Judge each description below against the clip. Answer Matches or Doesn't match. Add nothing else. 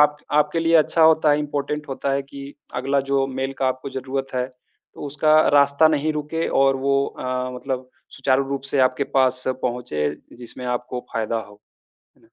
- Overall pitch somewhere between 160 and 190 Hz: Doesn't match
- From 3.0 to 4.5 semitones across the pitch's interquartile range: Doesn't match